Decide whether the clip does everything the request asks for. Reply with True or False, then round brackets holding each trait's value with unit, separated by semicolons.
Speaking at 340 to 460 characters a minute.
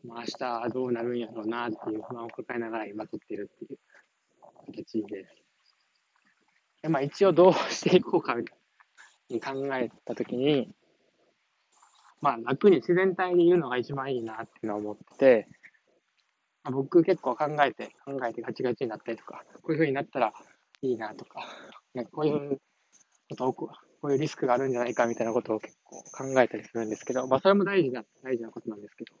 True (375 characters per minute)